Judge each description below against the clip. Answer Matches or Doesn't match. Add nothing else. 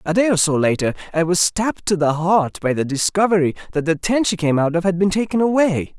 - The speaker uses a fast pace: Matches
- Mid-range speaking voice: Matches